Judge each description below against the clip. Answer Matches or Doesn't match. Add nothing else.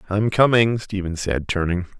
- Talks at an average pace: Matches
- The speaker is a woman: Doesn't match